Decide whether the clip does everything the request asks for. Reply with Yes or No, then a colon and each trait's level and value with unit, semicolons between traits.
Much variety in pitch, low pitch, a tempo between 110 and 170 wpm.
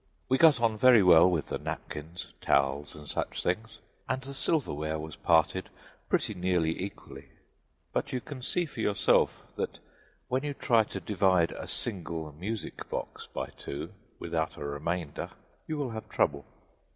Yes: wide, 7.5 semitones; very low, 90 Hz; average, 160 wpm